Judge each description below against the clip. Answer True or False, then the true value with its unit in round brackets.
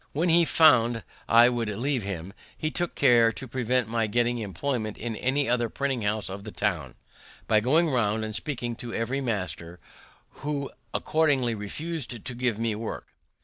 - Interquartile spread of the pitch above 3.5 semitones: True (4.0 semitones)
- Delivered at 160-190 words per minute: True (170 wpm)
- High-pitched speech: False (120 Hz)